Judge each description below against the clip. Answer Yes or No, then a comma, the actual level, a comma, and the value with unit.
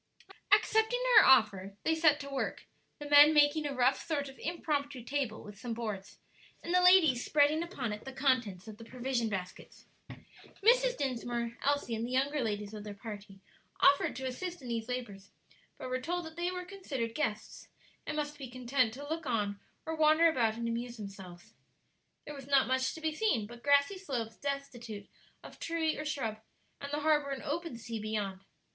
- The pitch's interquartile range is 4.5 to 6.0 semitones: Yes, average, 5.1 semitones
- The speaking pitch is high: Yes, very high, 265 Hz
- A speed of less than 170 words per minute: No, average, 190 wpm